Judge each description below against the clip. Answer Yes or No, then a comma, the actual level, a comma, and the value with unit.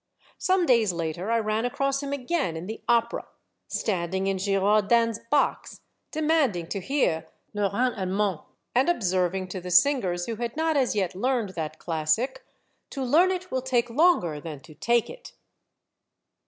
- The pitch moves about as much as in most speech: No, wide, 6.3 semitones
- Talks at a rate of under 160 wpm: No, average, 170 wpm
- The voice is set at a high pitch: Yes, high, 220 Hz